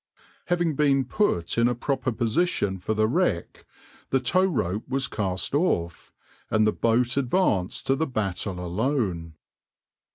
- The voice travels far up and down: Yes, wide, 6.4 semitones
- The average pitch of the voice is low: Yes, low, 120 Hz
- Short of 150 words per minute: Yes, average, 140 wpm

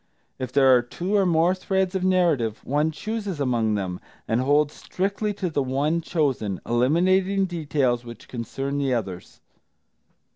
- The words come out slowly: No, average, 150 wpm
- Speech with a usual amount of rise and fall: No, wide, 6.9 semitones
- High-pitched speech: No, medium, 145 Hz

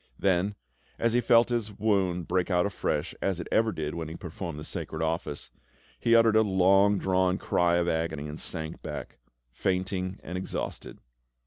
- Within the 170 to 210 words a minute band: Yes, average, 175 wpm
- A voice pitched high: No, very low, 95 Hz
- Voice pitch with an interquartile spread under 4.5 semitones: Yes, average, 3.3 semitones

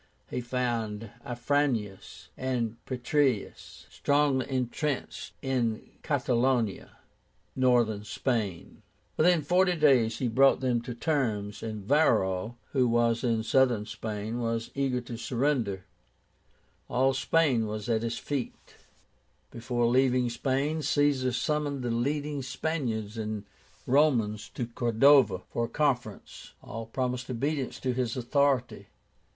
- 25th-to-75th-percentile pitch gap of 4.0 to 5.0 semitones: No, average, 3.2 semitones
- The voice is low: Yes, low, 125 Hz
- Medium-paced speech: No, slow, 120 wpm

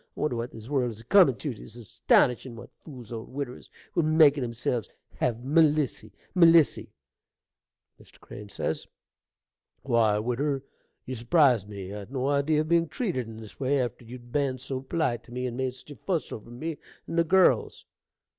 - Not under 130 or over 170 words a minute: No, average, 180 wpm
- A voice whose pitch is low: Yes, low, 130 Hz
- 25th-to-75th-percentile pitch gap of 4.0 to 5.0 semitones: Yes, average, 4.4 semitones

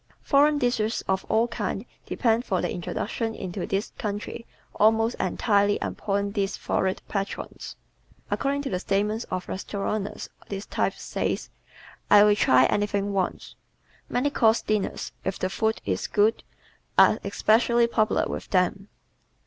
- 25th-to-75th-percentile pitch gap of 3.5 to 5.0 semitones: No, narrow, 2.5 semitones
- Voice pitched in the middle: No, high, 205 Hz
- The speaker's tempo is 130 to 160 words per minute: Yes, average, 140 wpm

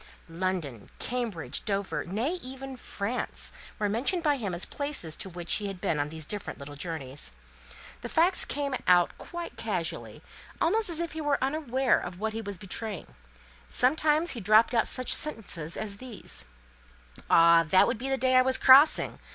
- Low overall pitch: No, high, 220 Hz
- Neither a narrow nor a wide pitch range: No, wide, 7.2 semitones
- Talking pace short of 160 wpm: No, average, 175 wpm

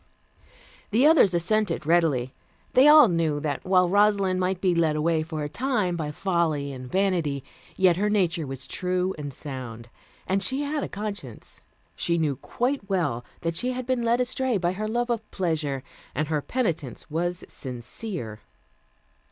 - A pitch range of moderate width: No, wide, 5.8 semitones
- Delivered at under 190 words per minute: Yes, average, 165 wpm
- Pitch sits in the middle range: Yes, medium, 175 Hz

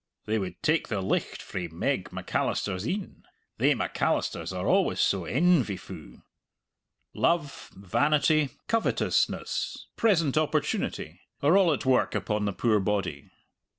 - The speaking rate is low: Yes, slow, 130 wpm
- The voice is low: Yes, low, 130 Hz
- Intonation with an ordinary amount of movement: No, wide, 8.2 semitones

